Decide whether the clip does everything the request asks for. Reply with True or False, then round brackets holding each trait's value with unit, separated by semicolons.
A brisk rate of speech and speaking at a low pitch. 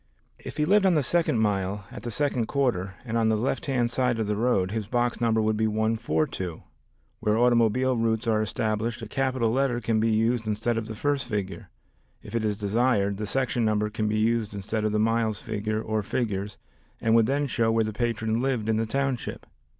True (210 wpm; 115 Hz)